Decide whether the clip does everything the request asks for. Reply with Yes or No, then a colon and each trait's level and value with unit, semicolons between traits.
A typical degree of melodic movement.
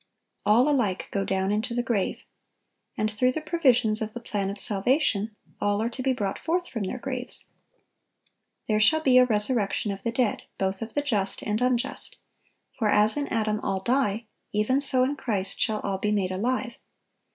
Yes: average, 3.6 semitones